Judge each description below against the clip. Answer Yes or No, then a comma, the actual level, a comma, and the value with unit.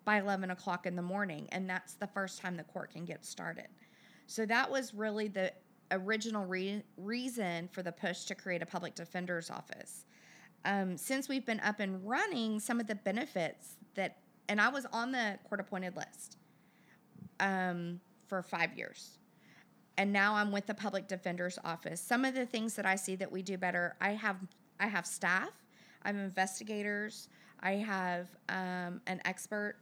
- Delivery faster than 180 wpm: No, average, 175 wpm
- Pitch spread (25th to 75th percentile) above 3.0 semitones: No, narrow, 2.6 semitones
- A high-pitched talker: Yes, high, 195 Hz